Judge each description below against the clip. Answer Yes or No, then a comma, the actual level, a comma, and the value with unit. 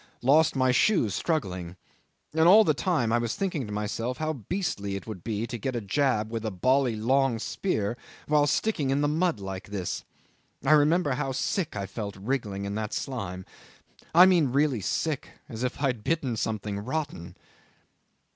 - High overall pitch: No, low, 125 Hz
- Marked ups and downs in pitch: Yes, wide, 6.2 semitones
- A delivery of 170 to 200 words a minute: Yes, average, 180 wpm